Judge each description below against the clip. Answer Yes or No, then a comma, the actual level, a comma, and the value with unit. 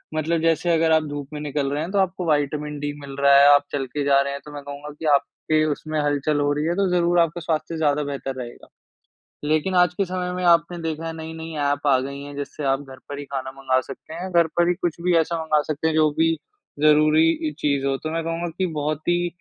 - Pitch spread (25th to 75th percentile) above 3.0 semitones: No, average, 2.7 semitones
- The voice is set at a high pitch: No, medium, 155 Hz